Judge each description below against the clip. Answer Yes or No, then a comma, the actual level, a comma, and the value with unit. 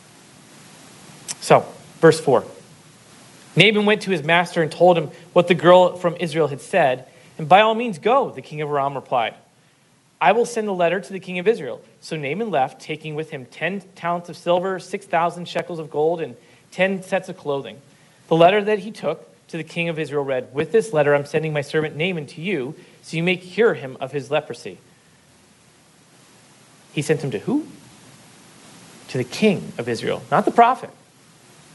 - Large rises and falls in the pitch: No, average, 3.5 semitones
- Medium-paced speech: Yes, average, 185 wpm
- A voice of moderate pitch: Yes, medium, 170 Hz